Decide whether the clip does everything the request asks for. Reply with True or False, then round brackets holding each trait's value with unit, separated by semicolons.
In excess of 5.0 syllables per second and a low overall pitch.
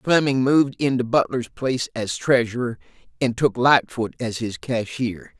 False (4.7 syllables/s; 120 Hz)